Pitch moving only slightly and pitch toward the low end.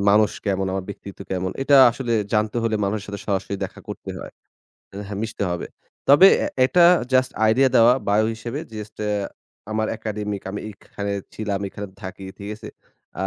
Yes: narrow, 2.1 semitones; low, 105 Hz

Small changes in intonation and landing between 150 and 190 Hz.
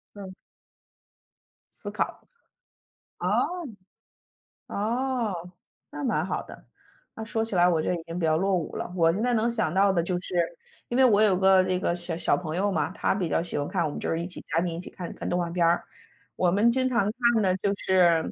No: average, 3.4 semitones; medium, 185 Hz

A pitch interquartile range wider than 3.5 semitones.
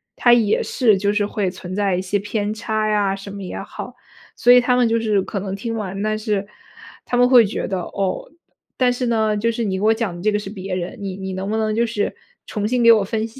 No: average, 2.7 semitones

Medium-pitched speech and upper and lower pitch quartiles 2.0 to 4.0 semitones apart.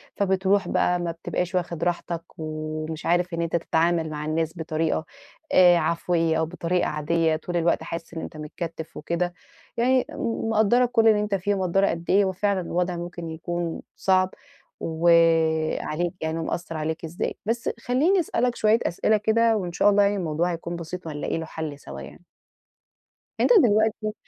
Yes: medium, 175 Hz; average, 3.6 semitones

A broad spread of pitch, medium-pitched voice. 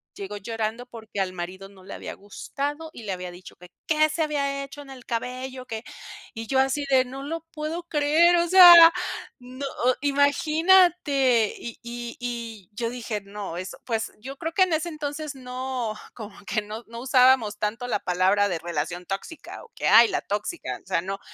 No: wide, 5.7 semitones; high, 245 Hz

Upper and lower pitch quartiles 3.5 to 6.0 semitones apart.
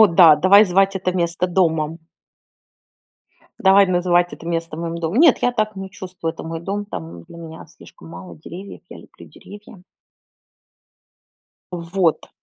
No: average, 2.8 semitones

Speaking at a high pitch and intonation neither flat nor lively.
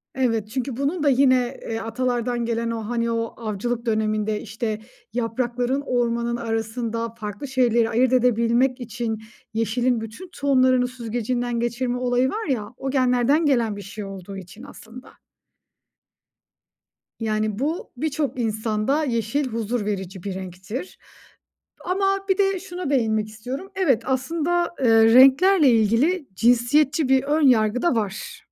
Yes: high, 240 Hz; average, 3.2 semitones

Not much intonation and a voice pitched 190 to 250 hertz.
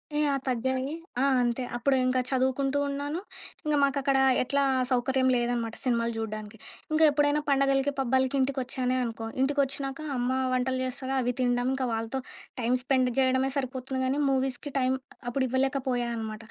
No: narrow, 1.8 semitones; very high, 260 Hz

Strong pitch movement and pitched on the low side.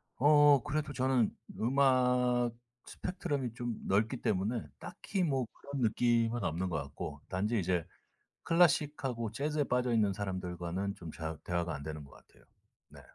Yes: wide, 6.3 semitones; low, 120 Hz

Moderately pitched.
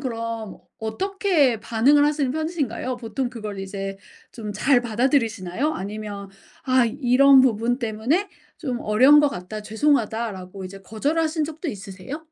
No: high, 235 Hz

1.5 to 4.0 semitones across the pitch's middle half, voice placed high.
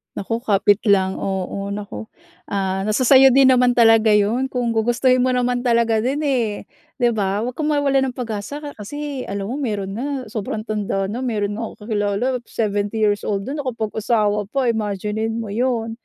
Yes: average, 3.5 semitones; high, 225 Hz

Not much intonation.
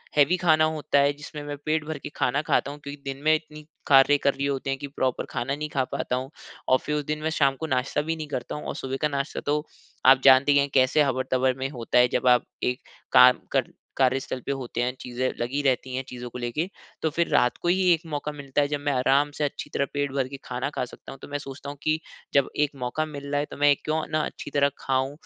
Yes: narrow, 2.2 semitones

